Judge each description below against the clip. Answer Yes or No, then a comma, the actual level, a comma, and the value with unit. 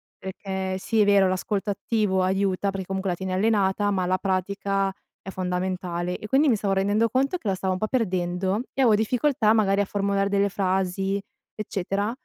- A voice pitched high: Yes, high, 195 Hz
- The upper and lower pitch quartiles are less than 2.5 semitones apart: Yes, narrow, 1.9 semitones